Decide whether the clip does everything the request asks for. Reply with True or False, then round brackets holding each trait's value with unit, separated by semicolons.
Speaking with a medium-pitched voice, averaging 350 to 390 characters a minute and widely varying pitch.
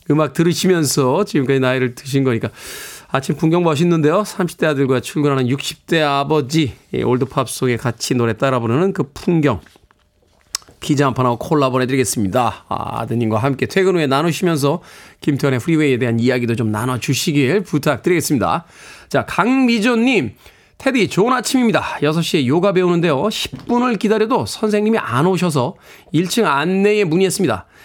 True (150 Hz; 355 characters per minute; 5.9 semitones)